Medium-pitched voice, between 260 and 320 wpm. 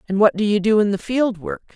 No: high, 210 Hz; fast, 305 wpm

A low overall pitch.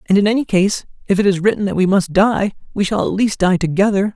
No: high, 195 Hz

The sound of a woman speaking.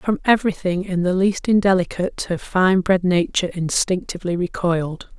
Yes: female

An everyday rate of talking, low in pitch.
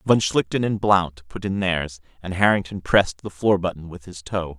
No: fast, 210 wpm; very low, 95 Hz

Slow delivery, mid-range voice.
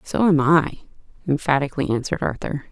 Yes: slow, 130 wpm; medium, 145 Hz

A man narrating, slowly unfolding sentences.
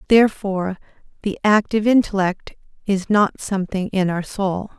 No: female; slow, 125 wpm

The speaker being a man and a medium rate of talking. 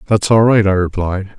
No: male; fast, 215 wpm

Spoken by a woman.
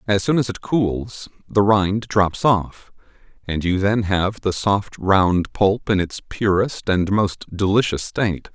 No: male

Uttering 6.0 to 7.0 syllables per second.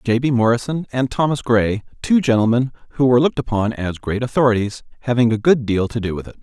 Yes: 6.3 syllables/s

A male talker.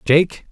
Yes: male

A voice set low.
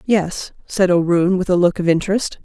No: medium, 185 Hz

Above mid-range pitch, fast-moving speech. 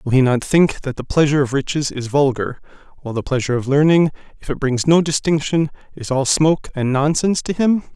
No: medium, 145 Hz; fast, 210 wpm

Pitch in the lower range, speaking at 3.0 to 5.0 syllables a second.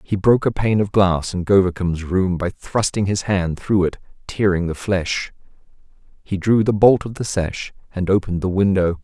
Yes: very low, 95 Hz; 4.9 syllables/s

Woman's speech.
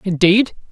No: male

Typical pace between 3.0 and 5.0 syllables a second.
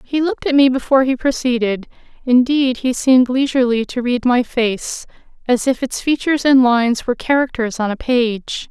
No: 5.4 syllables/s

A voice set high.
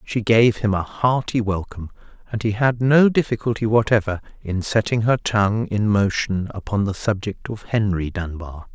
No: low, 105 Hz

